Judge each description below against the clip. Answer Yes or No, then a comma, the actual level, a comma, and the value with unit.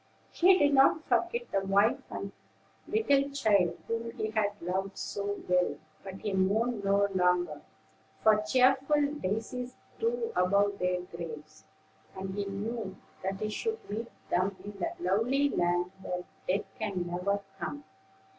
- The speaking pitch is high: Yes, high, 200 Hz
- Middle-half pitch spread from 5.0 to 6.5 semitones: Yes, average, 5.3 semitones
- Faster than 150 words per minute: No, average, 145 wpm